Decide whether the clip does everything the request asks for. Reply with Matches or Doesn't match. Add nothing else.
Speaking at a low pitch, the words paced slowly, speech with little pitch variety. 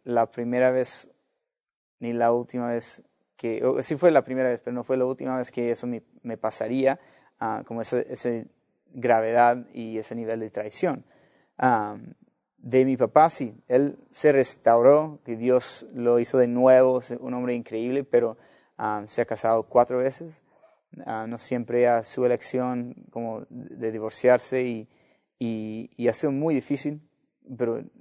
Doesn't match